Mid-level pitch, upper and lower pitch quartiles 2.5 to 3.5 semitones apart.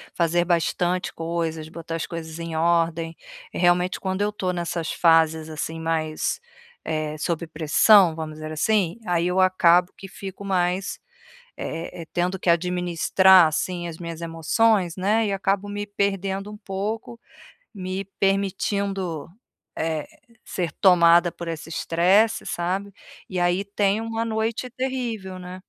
Yes: medium, 180 Hz; average, 2.9 semitones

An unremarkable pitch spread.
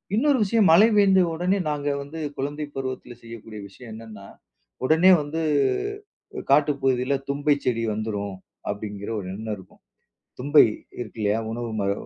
No: wide, 5.9 semitones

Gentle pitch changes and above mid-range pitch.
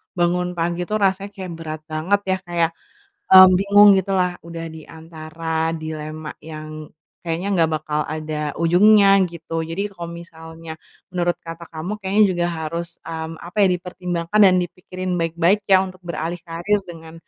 No: narrow, 2.2 semitones; medium, 170 Hz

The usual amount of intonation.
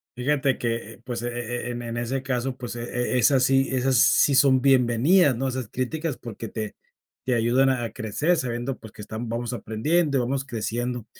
No: narrow, 2.3 semitones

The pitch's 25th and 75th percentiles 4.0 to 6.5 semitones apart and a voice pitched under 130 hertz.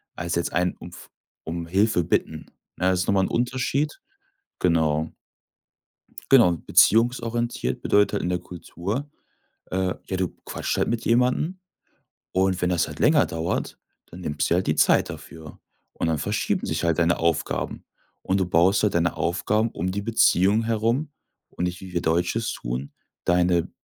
Yes: average, 4.7 semitones; very low, 90 Hz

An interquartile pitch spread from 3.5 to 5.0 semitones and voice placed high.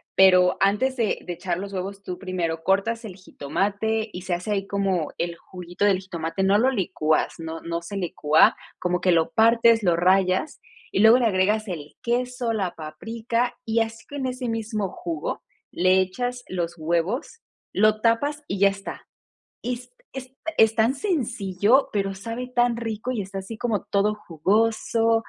Yes: average, 4.0 semitones; high, 200 Hz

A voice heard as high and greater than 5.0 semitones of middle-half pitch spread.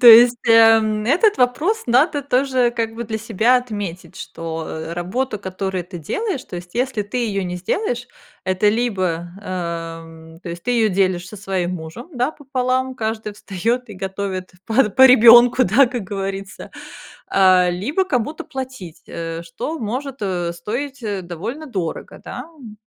Yes: high, 215 Hz; wide, 5.4 semitones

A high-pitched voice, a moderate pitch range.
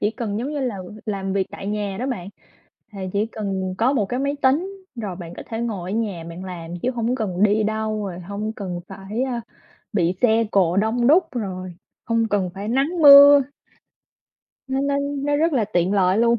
Yes: high, 215 Hz; average, 4.8 semitones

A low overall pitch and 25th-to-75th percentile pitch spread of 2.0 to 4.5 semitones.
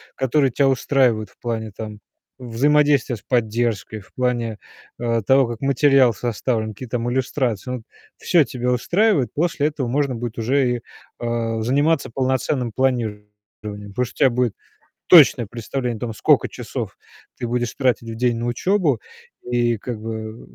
Yes: low, 120 Hz; average, 2.8 semitones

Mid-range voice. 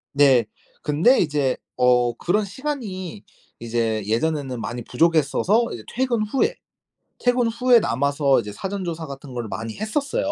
Yes: medium, 155 Hz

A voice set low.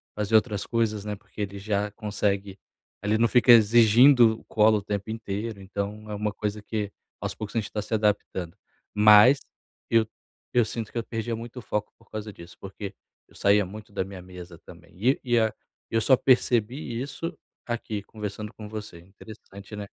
Yes: low, 105 Hz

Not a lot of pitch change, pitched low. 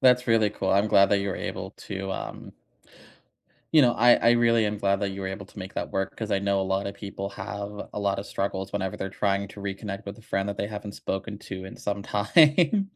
Yes: narrow, 1.7 semitones; low, 100 Hz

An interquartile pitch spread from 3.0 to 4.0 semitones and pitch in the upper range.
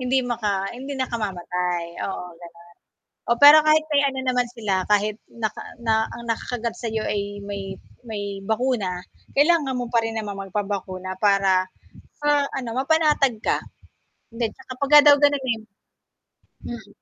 No: average, 4.6 semitones; high, 230 Hz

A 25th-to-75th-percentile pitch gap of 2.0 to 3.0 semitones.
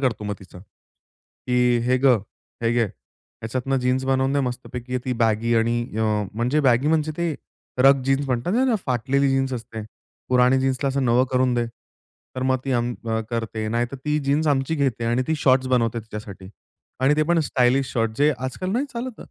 Yes: narrow, 2.5 semitones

